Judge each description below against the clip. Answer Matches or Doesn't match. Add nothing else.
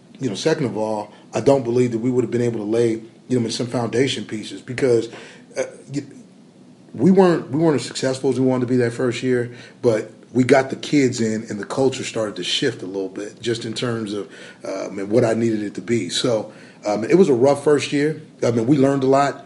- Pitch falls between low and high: Doesn't match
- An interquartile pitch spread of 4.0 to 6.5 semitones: Doesn't match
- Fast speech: Matches